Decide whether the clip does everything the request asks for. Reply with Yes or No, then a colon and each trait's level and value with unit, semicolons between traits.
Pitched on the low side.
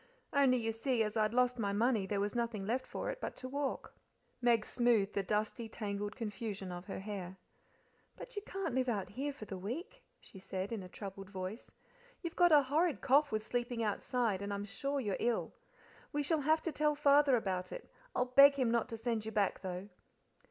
No: high, 230 Hz